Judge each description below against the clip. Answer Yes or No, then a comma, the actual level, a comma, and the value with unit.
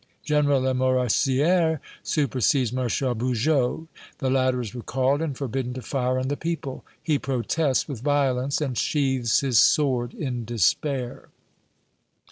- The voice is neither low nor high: No, low, 130 Hz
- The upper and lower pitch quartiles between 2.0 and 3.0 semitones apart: Yes, narrow, 2.4 semitones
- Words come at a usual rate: No, slow, 125 wpm